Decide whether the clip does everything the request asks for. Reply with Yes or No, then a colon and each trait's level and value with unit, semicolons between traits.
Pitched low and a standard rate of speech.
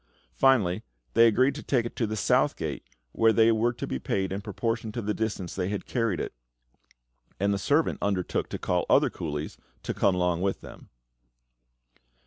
Yes: low, 105 Hz; average, 185 wpm